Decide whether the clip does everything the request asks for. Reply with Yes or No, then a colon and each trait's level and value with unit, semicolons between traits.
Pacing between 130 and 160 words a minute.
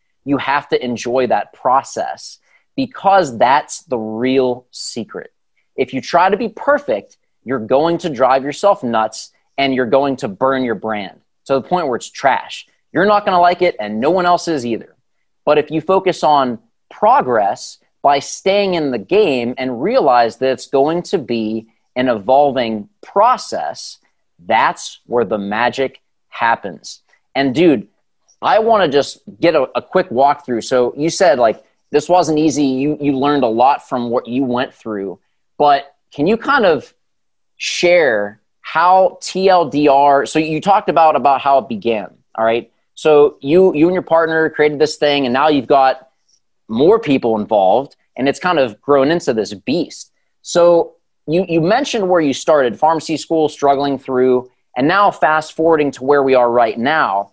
No: average, 175 wpm